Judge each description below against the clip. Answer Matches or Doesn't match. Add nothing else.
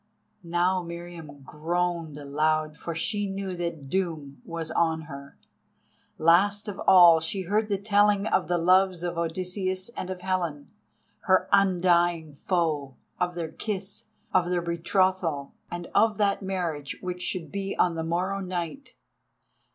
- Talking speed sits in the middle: Matches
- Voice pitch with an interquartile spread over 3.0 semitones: Doesn't match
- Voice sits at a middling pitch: Matches